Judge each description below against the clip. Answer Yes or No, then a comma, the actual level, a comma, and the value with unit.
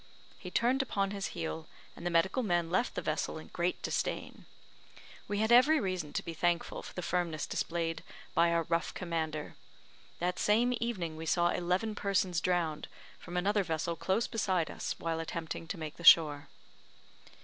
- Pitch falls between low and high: Yes, medium, 175 Hz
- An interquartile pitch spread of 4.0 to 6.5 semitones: No, average, 3.2 semitones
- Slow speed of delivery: No, average, 170 wpm